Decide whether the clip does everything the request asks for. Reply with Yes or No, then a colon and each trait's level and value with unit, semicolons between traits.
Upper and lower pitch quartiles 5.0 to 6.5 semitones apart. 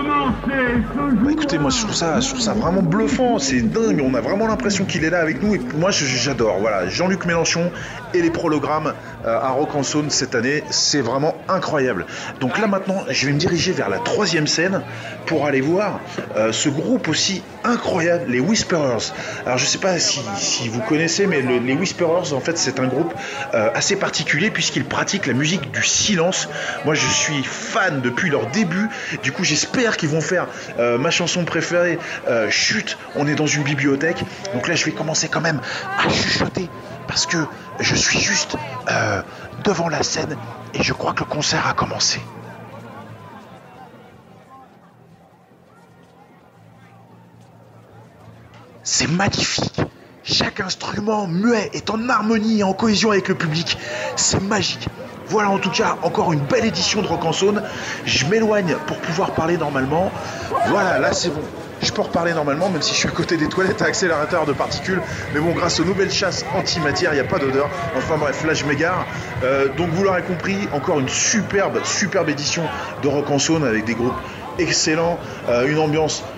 Yes: average, 5.3 semitones